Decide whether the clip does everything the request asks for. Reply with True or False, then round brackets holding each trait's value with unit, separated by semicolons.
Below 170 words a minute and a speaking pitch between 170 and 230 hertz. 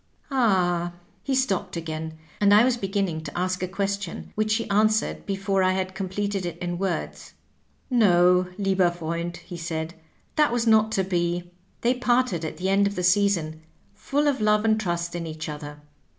False (180 wpm; 190 Hz)